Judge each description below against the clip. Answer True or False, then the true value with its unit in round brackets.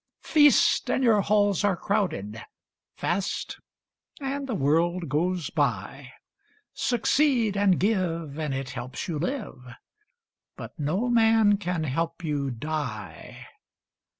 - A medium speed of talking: False (115 wpm)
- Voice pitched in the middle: True (180 Hz)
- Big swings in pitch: True (6.3 semitones)